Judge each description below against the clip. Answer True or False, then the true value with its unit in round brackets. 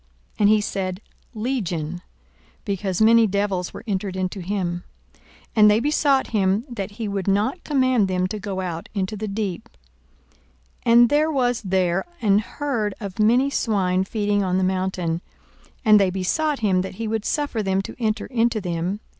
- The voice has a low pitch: False (205 Hz)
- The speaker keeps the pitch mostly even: False (3.3 semitones)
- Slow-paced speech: False (170 wpm)